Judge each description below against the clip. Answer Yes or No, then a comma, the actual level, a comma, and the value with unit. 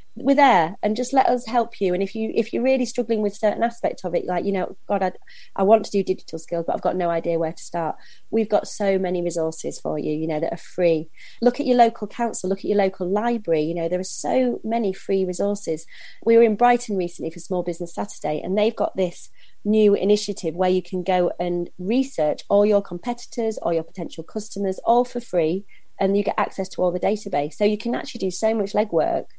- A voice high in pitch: Yes, high, 195 Hz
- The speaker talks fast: Yes, fast, 235 wpm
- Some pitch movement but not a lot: Yes, average, 4.2 semitones